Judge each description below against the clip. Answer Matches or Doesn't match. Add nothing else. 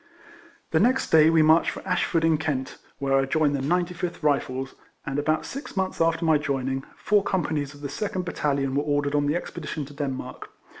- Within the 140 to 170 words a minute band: Doesn't match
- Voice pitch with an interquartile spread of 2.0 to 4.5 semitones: Matches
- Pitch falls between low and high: Matches